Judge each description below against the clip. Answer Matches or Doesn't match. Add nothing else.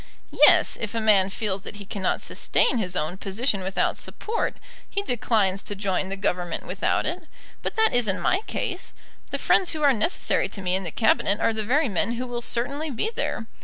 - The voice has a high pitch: Matches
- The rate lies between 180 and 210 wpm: Matches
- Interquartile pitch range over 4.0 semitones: Matches